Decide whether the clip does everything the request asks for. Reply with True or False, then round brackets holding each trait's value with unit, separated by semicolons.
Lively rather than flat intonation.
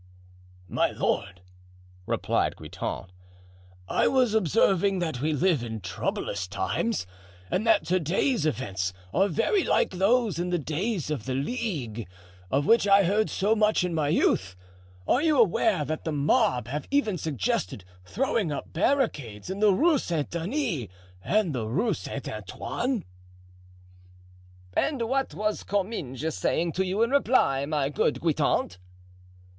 True (7.8 semitones)